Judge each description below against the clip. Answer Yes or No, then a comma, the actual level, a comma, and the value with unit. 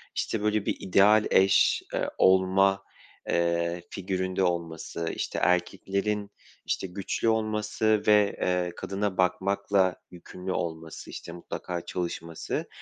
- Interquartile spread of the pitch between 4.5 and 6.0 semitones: No, narrow, 2.5 semitones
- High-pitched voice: No, very low, 95 Hz